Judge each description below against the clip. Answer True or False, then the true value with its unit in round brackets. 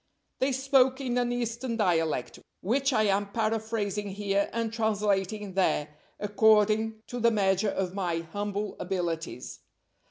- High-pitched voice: True (210 Hz)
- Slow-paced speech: True (130 wpm)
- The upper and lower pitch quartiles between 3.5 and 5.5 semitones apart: False (3.1 semitones)